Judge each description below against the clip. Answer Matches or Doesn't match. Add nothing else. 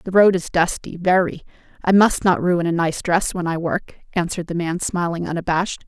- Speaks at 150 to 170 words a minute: Doesn't match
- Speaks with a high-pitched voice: Doesn't match